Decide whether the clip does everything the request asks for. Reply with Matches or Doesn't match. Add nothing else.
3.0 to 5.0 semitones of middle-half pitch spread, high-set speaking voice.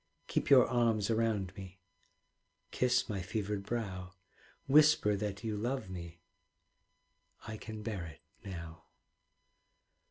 Doesn't match